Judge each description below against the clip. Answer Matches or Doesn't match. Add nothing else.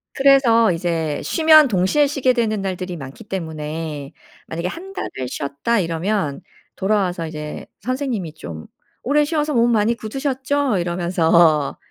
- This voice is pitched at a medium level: Doesn't match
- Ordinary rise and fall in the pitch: Doesn't match